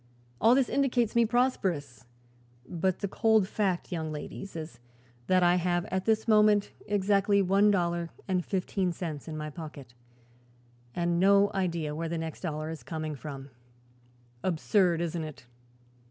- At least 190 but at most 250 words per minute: No, average, 150 wpm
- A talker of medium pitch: Yes, medium, 175 Hz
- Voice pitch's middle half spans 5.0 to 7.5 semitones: No, average, 4.0 semitones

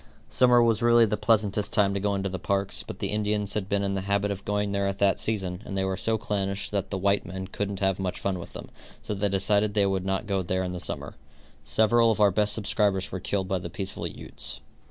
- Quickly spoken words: Yes, fast, 250 wpm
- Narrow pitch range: Yes, narrow, 1.5 semitones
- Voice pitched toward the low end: Yes, low, 100 Hz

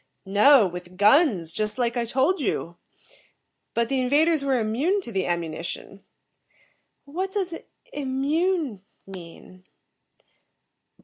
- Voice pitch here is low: No, high, 240 Hz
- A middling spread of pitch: No, wide, 7.3 semitones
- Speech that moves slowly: Yes, slow, 110 wpm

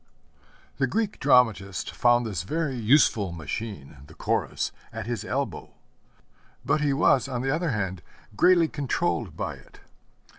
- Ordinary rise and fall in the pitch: No, wide, 6.6 semitones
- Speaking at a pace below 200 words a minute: Yes, average, 140 wpm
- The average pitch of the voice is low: Yes, low, 120 Hz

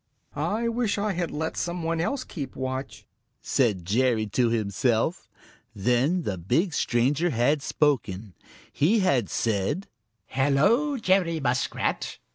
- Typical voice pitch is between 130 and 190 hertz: Yes, medium, 140 Hz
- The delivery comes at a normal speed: No, slow, 125 wpm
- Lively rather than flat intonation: Yes, wide, 7.1 semitones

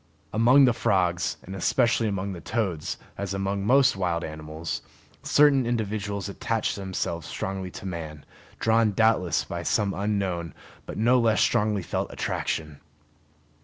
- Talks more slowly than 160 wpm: Yes, slow, 135 wpm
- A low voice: Yes, low, 100 Hz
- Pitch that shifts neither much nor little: Yes, average, 4.4 semitones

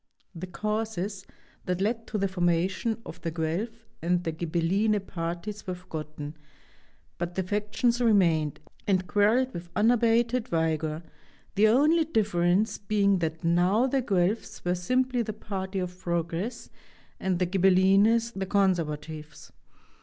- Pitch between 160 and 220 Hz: Yes, high, 190 Hz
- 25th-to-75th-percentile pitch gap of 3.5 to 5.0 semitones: Yes, average, 4.1 semitones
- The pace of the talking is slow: Yes, slow, 130 wpm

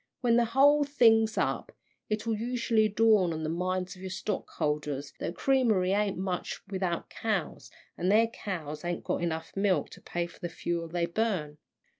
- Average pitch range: Yes, average, 4.6 semitones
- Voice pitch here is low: No, high, 190 Hz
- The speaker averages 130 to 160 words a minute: No, average, 175 wpm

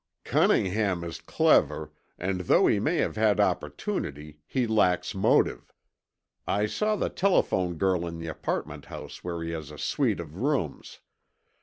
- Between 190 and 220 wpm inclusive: No, average, 150 wpm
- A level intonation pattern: No, average, 4.2 semitones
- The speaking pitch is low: Yes, very low, 90 Hz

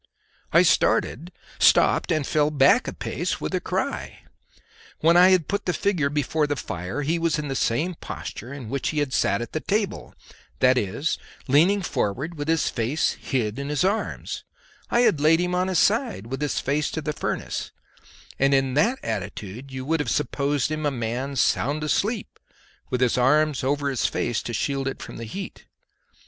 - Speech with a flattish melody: No, average, 3.9 semitones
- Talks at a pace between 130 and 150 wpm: No, average, 190 wpm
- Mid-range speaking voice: Yes, medium, 145 Hz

